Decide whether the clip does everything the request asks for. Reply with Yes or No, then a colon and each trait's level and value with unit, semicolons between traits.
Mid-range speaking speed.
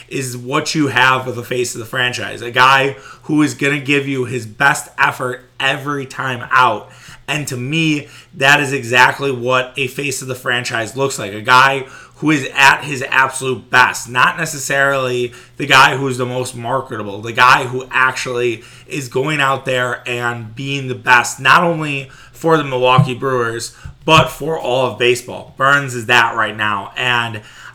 Yes: average, 180 wpm